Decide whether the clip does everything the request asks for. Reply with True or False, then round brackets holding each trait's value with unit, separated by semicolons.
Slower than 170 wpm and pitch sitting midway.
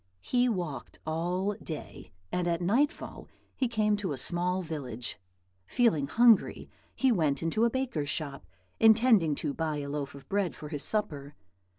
True (160 wpm; 175 Hz)